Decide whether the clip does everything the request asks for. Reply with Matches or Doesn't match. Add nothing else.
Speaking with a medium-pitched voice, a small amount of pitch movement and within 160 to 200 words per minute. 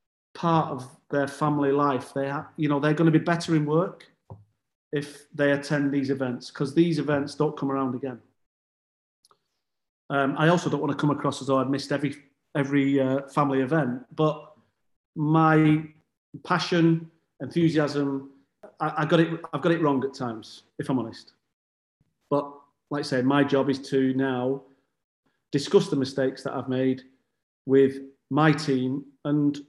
Matches